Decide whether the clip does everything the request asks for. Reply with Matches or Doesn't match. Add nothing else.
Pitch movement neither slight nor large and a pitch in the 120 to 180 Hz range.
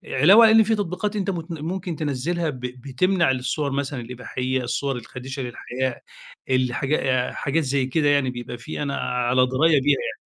Matches